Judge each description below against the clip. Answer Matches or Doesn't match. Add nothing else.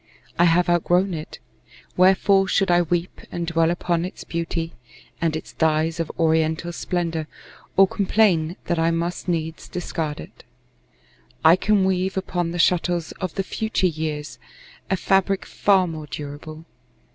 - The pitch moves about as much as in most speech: Doesn't match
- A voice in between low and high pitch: Matches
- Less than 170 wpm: Matches